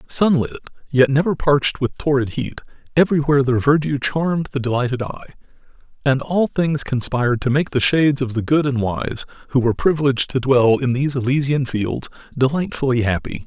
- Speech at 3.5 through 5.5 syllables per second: No, 5.9 syllables/s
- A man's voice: Yes, male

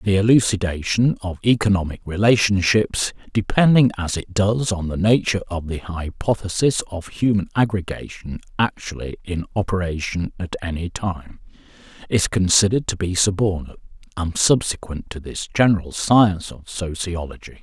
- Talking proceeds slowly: Yes, slow, 125 wpm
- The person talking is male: Yes, male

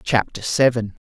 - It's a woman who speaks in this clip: No, male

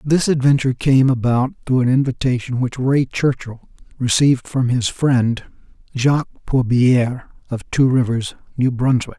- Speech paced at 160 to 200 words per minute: No, slow, 135 wpm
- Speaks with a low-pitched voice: Yes, low, 130 Hz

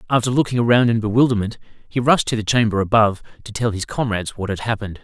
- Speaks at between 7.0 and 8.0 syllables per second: Yes, 7.1 syllables/s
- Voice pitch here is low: Yes, low, 110 Hz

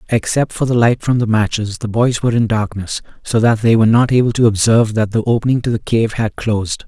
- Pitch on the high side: No, low, 115 Hz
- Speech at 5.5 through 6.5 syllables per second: Yes, 6.0 syllables/s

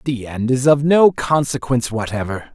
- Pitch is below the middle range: Yes, low, 130 Hz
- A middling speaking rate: Yes, average, 165 wpm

